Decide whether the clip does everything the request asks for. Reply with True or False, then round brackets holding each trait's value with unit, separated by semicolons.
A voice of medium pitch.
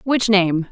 False (200 Hz)